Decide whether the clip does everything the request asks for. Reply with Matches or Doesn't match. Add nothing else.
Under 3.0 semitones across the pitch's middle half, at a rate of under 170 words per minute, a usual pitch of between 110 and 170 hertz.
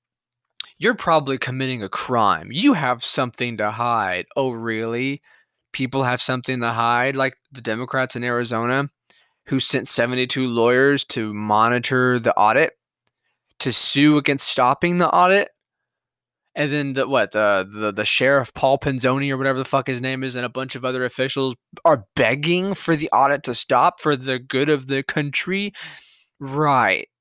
Matches